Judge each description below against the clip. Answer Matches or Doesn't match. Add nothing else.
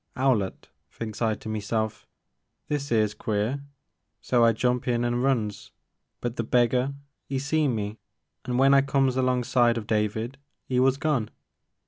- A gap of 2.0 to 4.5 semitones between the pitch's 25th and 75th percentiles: Matches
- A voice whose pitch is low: Matches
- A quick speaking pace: Doesn't match